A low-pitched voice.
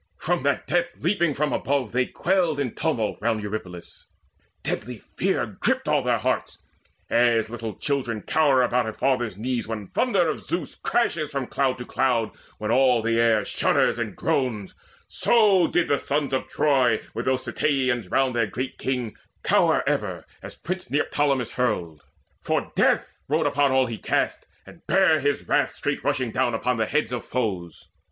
Yes: low, 130 Hz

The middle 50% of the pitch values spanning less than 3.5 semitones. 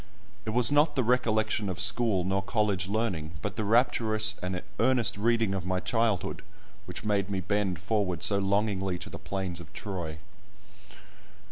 Yes: average, 3.0 semitones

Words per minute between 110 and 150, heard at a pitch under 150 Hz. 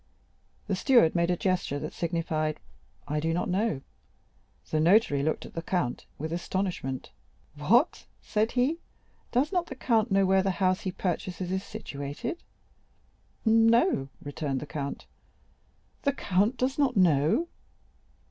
No: average, 140 wpm; medium, 185 Hz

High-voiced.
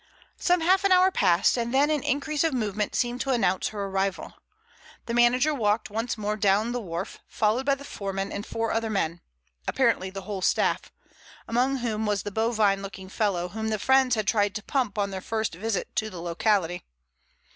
Yes: high, 215 Hz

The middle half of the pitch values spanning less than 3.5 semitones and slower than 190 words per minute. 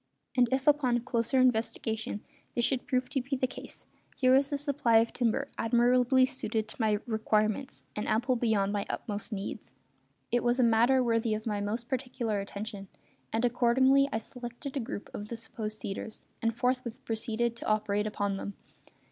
Yes: average, 2.8 semitones; average, 175 wpm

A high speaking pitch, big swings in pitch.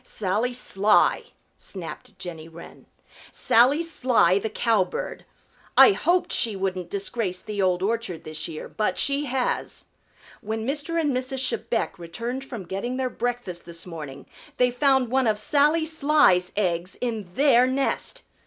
Yes: high, 230 Hz; wide, 6.2 semitones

